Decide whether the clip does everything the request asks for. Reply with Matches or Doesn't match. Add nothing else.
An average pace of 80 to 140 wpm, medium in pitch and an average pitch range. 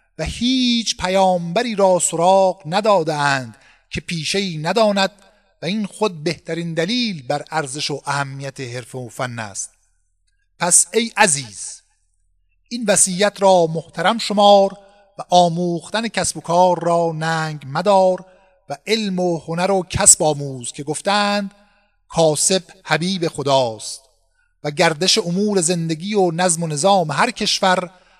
Matches